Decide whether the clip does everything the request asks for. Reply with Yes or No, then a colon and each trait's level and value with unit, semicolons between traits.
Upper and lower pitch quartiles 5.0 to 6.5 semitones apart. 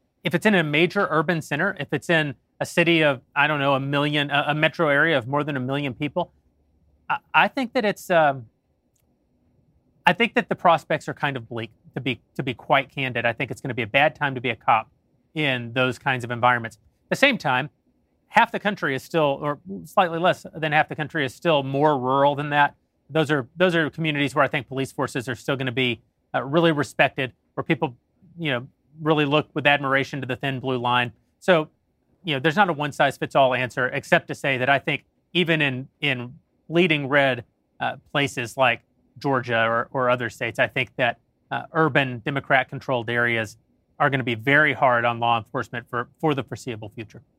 No: average, 3.7 semitones